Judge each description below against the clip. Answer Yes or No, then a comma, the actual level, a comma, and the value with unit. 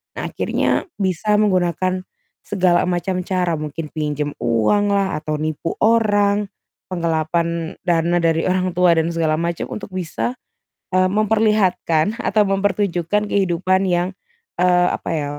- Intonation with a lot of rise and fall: No, average, 3.2 semitones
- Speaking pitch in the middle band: Yes, medium, 180 Hz